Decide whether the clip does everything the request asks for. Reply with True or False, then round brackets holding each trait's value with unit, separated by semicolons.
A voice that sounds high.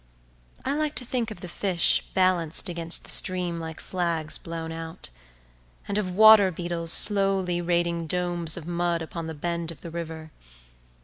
False (175 Hz)